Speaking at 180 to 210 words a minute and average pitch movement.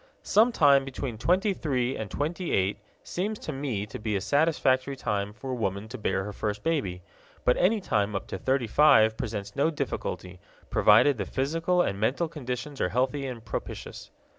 No: average, 185 wpm; wide, 6.1 semitones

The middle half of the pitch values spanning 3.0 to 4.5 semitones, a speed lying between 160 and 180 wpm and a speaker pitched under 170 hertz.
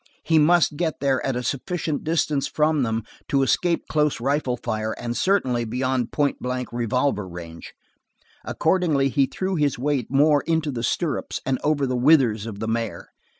Yes: average, 4.1 semitones; average, 170 wpm; low, 135 Hz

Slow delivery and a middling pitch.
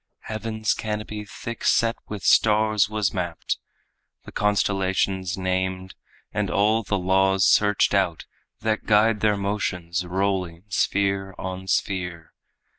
No: slow, 115 wpm; low, 100 Hz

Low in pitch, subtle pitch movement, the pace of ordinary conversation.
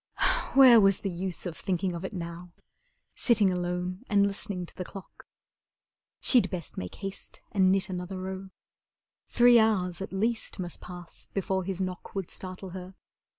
No: high, 190 Hz; narrow, 1.7 semitones; average, 160 wpm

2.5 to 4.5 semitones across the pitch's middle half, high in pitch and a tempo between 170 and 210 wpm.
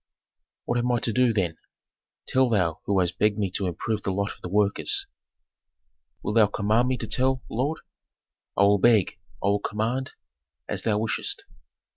No: average, 3.3 semitones; low, 105 Hz; average, 175 wpm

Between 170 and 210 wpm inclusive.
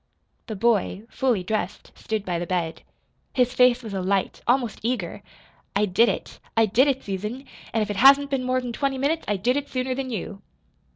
Yes: average, 195 wpm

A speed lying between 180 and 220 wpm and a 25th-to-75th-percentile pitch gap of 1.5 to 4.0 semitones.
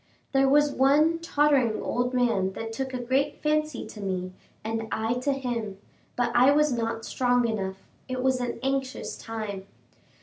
No: average, 165 wpm; average, 3.3 semitones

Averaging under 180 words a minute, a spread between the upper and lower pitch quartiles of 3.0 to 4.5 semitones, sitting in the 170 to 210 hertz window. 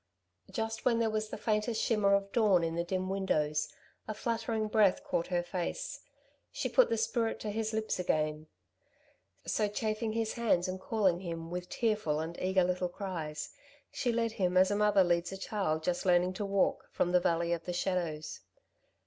No: average, 185 wpm; average, 3.8 semitones; high, 190 Hz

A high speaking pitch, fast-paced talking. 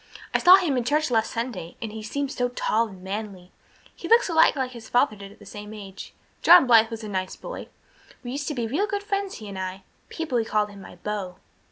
Yes: high, 225 Hz; fast, 240 wpm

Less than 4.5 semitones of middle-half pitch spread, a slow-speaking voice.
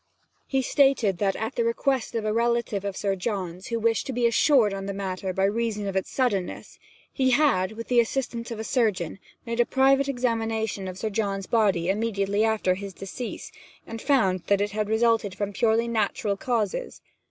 No: average, 3.1 semitones; average, 190 wpm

